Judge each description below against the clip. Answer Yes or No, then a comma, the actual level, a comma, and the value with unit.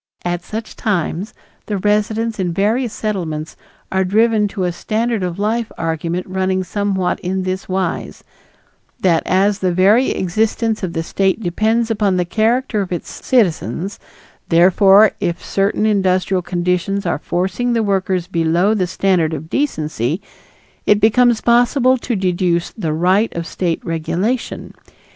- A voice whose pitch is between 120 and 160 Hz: No, high, 190 Hz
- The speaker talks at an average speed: Yes, average, 145 wpm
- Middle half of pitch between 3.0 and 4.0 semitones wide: Yes, average, 3.6 semitones